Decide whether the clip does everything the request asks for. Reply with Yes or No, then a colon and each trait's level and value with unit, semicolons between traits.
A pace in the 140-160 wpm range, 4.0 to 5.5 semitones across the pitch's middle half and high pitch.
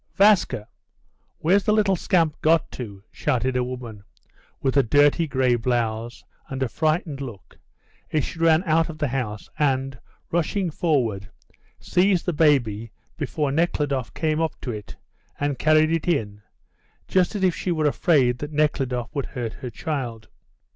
No: average, 155 wpm; average, 4.9 semitones; medium, 145 Hz